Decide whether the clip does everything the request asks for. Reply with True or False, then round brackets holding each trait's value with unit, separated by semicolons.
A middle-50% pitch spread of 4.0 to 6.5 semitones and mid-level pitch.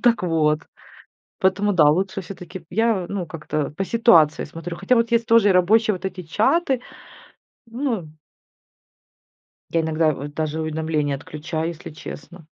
True (5.2 semitones; 175 Hz)